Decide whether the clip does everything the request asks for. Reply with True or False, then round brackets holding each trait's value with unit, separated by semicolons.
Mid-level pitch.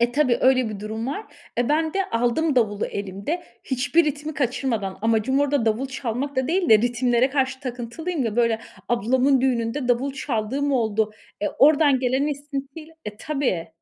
False (255 Hz)